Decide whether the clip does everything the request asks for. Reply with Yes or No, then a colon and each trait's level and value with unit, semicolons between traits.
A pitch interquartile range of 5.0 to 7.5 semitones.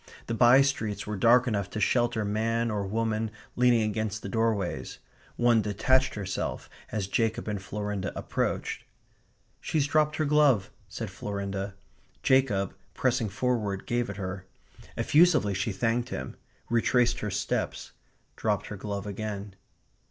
No: average, 3.3 semitones